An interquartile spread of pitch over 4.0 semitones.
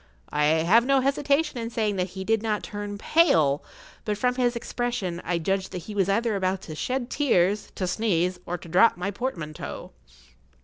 Yes: average, 5.0 semitones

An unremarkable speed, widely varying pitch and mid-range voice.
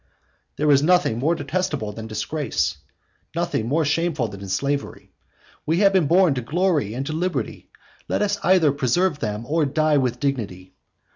Yes: average, 160 wpm; wide, 5.8 semitones; medium, 145 Hz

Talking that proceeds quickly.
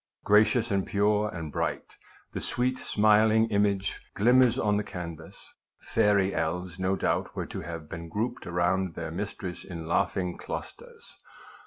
No: average, 150 wpm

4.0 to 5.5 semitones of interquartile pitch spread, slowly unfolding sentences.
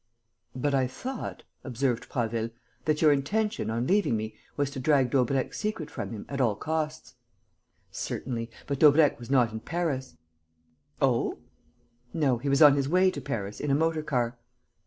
No: average, 4.3 semitones; average, 165 wpm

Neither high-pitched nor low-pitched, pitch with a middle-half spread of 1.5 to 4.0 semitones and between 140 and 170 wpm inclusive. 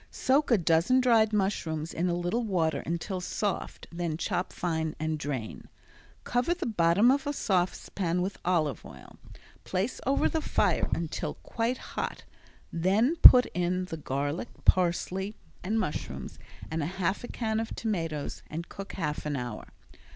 No: medium, 180 Hz; average, 5.2 semitones; average, 150 wpm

